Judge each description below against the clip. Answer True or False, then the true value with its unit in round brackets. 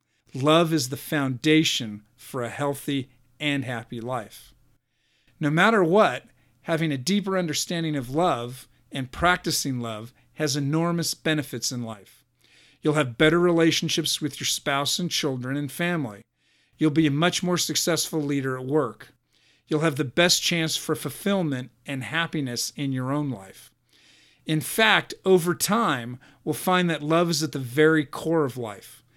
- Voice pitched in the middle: True (150 Hz)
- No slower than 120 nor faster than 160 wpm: True (155 wpm)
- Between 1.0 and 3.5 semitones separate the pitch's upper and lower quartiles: False (4.1 semitones)